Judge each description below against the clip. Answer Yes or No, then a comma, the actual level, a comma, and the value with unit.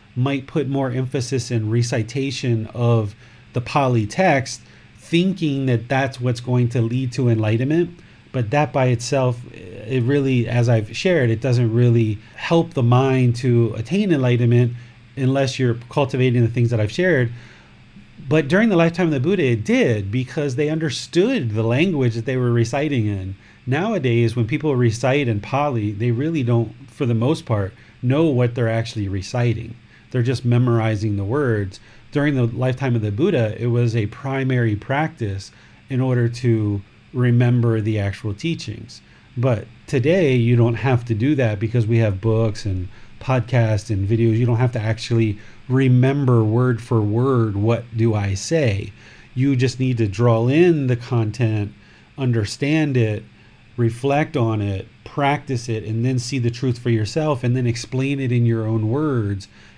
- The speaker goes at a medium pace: Yes, average, 165 wpm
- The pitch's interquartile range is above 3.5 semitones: No, average, 2.8 semitones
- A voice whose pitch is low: Yes, low, 120 Hz